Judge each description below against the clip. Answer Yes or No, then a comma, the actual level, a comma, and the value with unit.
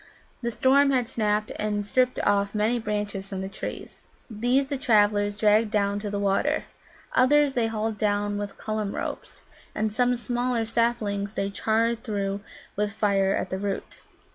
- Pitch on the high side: Yes, high, 210 Hz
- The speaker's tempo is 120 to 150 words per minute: No, average, 165 wpm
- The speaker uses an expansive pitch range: No, narrow, 2.6 semitones